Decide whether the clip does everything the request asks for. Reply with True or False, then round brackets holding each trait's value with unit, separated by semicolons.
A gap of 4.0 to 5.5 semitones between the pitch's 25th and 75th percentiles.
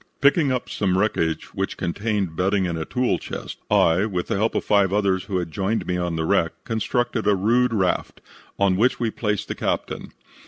False (3.6 semitones)